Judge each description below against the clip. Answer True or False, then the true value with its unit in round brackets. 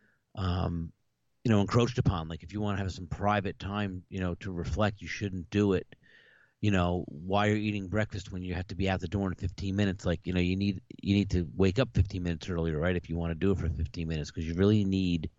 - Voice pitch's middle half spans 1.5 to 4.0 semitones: True (2.7 semitones)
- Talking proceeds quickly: True (255 wpm)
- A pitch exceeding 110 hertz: False (95 Hz)